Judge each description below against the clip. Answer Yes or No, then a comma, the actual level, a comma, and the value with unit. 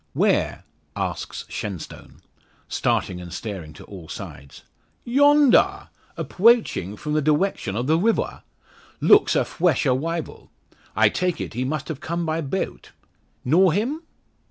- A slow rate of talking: Yes, slow, 130 wpm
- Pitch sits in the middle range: Yes, medium, 155 Hz